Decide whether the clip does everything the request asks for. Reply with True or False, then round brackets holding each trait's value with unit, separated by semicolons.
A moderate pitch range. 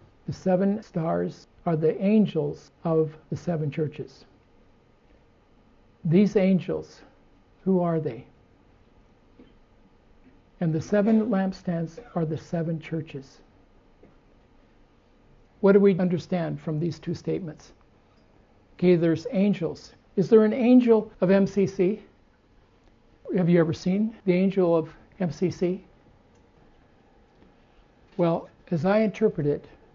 True (4.0 semitones)